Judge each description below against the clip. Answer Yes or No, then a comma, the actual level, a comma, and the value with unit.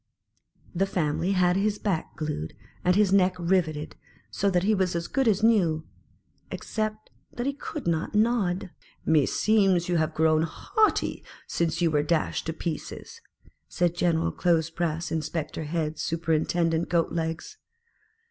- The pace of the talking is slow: No, average, 150 wpm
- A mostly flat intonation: No, average, 3.3 semitones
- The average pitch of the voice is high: No, medium, 170 Hz